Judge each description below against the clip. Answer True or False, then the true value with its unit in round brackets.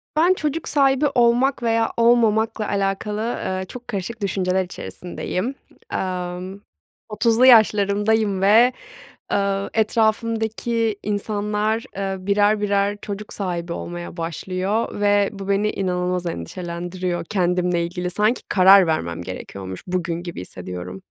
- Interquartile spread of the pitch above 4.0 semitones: False (3.6 semitones)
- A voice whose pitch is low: False (200 Hz)